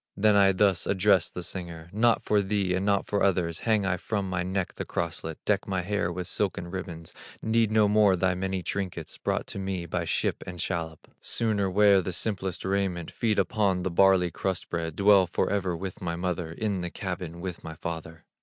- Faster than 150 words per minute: Yes, average, 200 wpm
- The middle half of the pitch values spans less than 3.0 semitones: Yes, narrow, 2.5 semitones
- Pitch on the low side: Yes, very low, 95 Hz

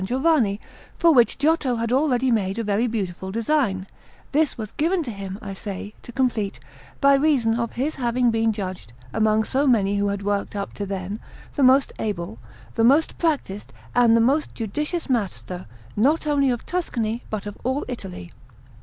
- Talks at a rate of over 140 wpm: Yes, average, 175 wpm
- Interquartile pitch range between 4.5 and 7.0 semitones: Yes, average, 5.1 semitones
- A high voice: Yes, high, 230 Hz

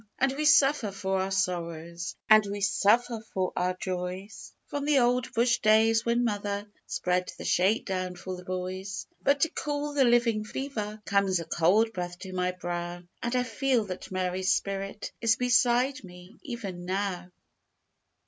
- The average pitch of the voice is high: Yes, high, 200 Hz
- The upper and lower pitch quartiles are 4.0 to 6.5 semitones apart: Yes, average, 4.6 semitones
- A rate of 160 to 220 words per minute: Yes, average, 165 wpm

